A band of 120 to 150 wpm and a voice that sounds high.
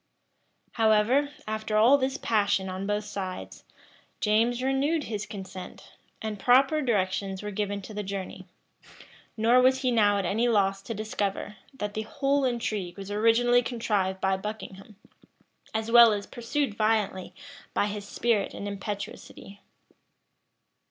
Yes: average, 140 wpm; high, 215 Hz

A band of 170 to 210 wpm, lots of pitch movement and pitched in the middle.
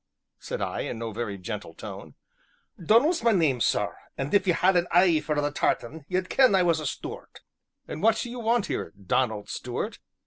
Yes: average, 200 wpm; wide, 7.1 semitones; medium, 170 Hz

